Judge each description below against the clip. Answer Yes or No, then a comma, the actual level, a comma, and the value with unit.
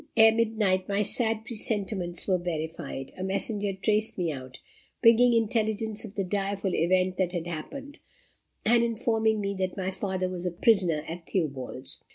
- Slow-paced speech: No, average, 160 wpm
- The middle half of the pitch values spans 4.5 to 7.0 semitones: No, average, 3.7 semitones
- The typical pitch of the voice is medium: No, high, 195 Hz